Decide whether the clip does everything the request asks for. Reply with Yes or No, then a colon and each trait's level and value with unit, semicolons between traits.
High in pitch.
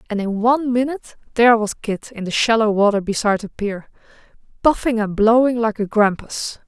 Yes: high, 220 Hz